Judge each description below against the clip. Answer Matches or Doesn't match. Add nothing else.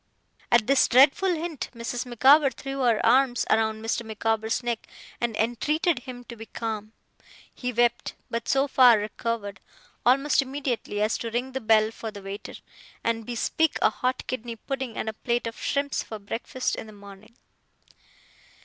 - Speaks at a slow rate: Doesn't match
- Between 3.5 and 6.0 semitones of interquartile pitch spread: Doesn't match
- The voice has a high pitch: Matches